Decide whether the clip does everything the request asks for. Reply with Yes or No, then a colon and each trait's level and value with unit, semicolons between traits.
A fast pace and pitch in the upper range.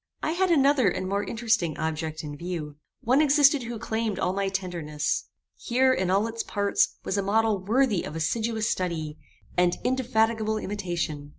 No: average, 165 wpm; high, 205 Hz